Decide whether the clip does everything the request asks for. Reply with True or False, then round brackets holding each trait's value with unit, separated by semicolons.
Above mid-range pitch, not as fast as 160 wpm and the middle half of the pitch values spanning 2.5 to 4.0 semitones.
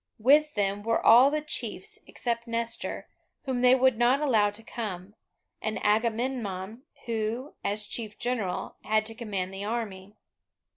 True (225 Hz; 145 wpm; 3.1 semitones)